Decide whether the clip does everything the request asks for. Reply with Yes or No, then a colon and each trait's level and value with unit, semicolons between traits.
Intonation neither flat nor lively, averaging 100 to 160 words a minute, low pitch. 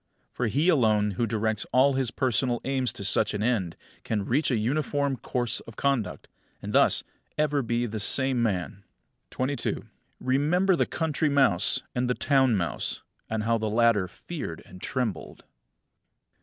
Yes: average, 4.1 semitones; average, 155 wpm; low, 120 Hz